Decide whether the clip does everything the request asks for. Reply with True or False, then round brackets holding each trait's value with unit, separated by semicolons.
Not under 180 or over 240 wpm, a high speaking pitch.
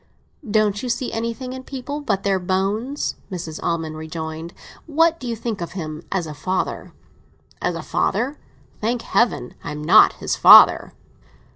False (160 wpm; 200 Hz)